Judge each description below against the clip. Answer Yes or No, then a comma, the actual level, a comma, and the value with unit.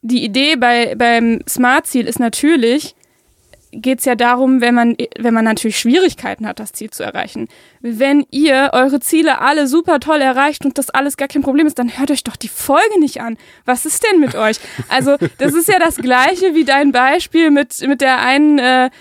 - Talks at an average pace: No, fast, 200 wpm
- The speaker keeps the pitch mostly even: No, average, 3.6 semitones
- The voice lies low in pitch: No, very high, 265 Hz